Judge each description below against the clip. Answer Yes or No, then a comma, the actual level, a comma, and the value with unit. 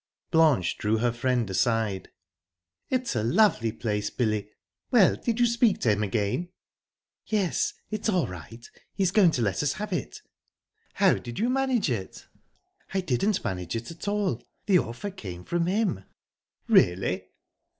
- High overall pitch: No, low, 125 Hz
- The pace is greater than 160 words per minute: No, average, 150 wpm